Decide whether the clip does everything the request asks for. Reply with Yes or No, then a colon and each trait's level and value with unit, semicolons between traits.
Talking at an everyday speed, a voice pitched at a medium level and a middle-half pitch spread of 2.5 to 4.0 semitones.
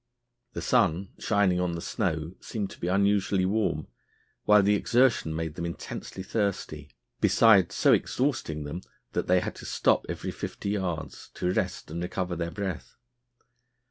No: average, 155 wpm; very low, 90 Hz; average, 3.3 semitones